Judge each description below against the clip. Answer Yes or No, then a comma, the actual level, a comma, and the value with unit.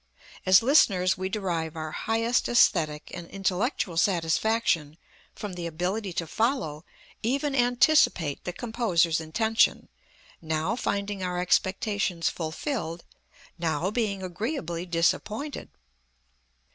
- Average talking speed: No, slow, 105 wpm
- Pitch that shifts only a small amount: No, average, 5.1 semitones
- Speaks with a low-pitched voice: No, medium, 185 Hz